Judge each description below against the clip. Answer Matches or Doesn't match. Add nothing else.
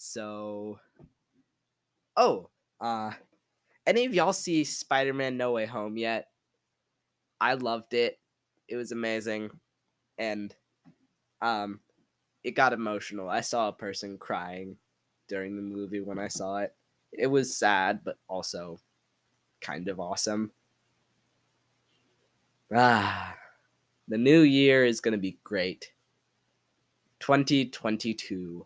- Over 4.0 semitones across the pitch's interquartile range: Doesn't match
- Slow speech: Matches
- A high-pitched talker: Doesn't match